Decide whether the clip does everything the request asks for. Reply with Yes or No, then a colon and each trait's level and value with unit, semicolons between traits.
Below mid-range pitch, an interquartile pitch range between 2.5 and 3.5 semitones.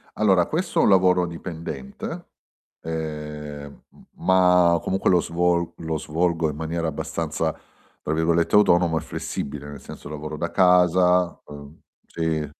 Yes: very low, 85 Hz; average, 2.8 semitones